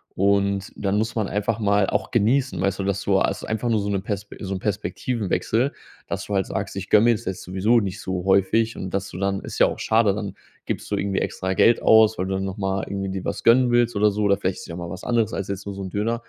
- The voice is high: No, low, 100 Hz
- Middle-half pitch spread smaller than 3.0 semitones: Yes, narrow, 2.4 semitones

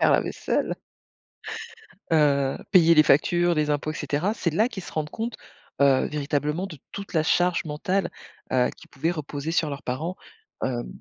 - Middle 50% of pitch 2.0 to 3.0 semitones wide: No, average, 3.4 semitones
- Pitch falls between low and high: Yes, medium, 155 Hz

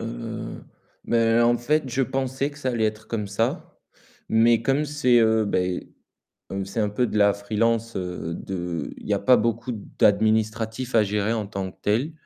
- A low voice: Yes, low, 110 Hz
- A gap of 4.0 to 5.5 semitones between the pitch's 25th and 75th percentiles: No, average, 2.9 semitones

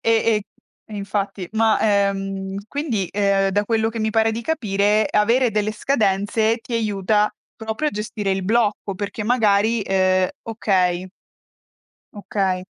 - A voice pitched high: Yes, high, 210 Hz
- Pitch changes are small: Yes, narrow, 2.3 semitones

